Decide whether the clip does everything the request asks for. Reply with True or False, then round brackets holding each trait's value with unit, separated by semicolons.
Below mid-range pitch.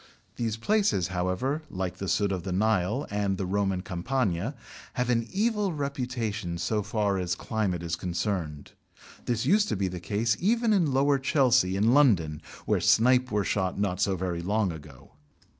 True (105 Hz)